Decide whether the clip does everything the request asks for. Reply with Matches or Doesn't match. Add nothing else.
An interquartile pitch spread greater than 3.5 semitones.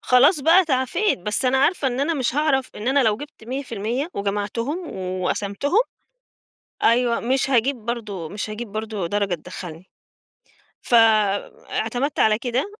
Matches